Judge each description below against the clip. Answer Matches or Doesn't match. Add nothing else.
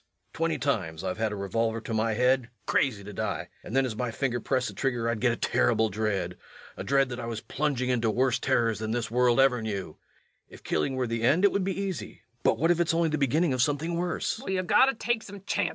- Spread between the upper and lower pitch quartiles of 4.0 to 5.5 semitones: Doesn't match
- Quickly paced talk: Matches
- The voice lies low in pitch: Matches